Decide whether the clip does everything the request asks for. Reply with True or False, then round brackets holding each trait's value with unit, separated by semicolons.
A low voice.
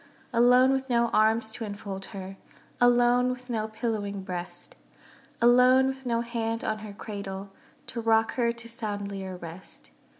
False (225 Hz)